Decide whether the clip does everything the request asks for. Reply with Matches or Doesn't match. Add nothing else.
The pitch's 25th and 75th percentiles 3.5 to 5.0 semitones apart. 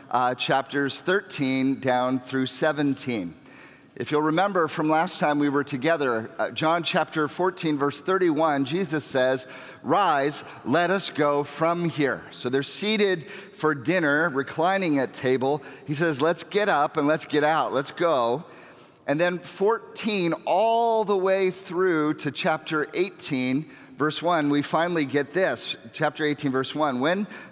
Matches